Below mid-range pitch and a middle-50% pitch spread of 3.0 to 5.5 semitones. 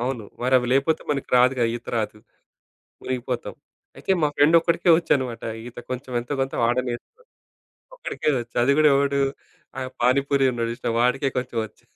No: low, 130 Hz; narrow, 2.6 semitones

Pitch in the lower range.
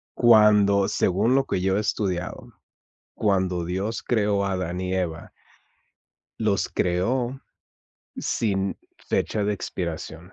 Yes: very low, 95 Hz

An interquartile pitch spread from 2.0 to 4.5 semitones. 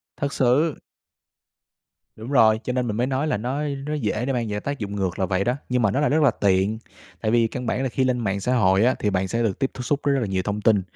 Yes: average, 4.2 semitones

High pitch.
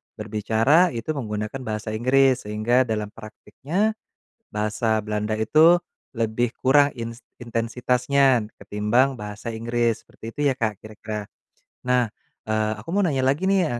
No: low, 115 Hz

